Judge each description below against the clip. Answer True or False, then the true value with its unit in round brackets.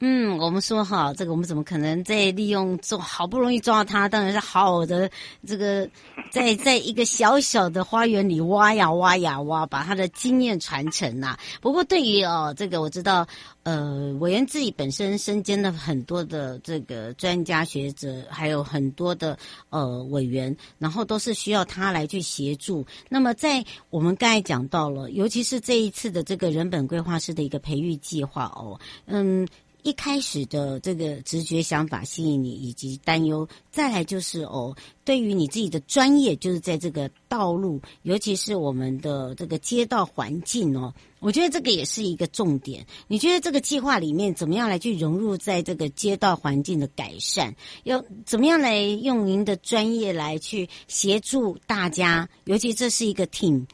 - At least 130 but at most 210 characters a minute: False (275 characters per minute)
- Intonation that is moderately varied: False (5.8 semitones)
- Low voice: False (180 Hz)